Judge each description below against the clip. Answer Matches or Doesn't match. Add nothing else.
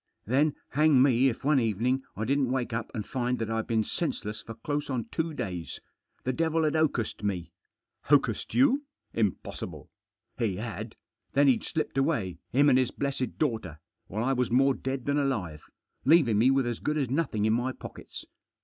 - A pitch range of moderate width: Matches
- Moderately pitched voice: Doesn't match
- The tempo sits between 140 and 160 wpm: Doesn't match